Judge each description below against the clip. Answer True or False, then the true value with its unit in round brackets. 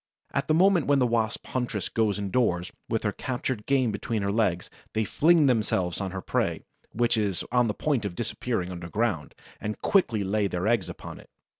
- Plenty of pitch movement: False (3.9 semitones)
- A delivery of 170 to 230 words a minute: True (190 wpm)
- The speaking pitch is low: True (110 Hz)